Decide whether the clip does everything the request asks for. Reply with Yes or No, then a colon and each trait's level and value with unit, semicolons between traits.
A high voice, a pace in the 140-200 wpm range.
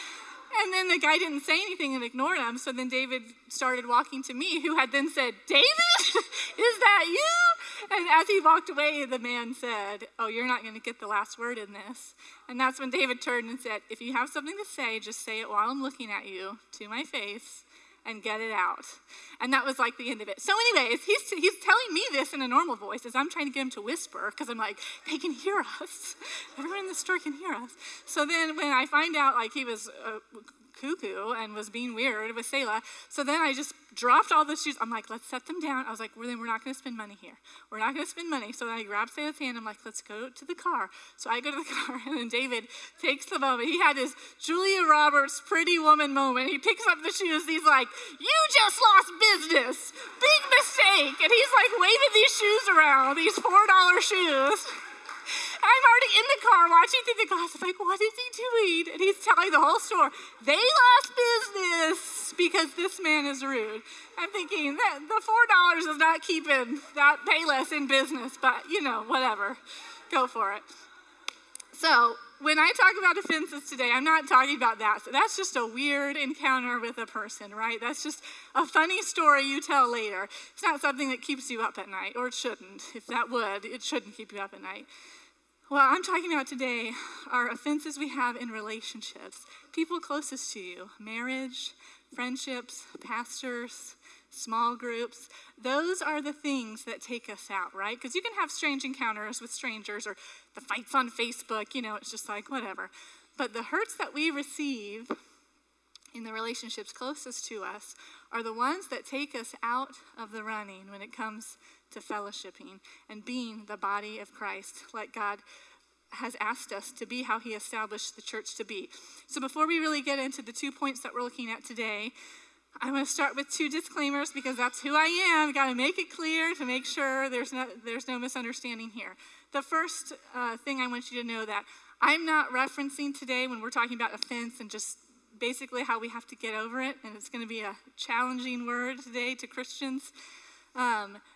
No: very high, 270 Hz; fast, 210 wpm